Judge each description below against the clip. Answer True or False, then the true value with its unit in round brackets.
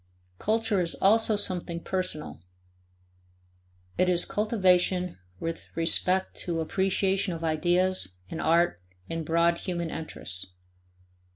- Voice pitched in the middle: True (175 Hz)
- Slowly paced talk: True (105 wpm)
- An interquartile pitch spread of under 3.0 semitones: True (2.4 semitones)